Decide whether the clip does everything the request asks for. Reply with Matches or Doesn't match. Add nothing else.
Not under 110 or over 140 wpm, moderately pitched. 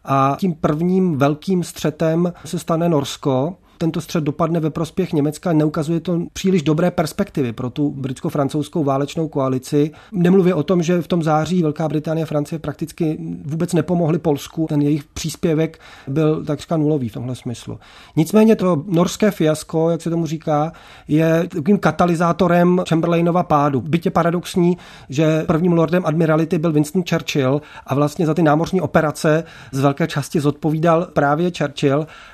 Doesn't match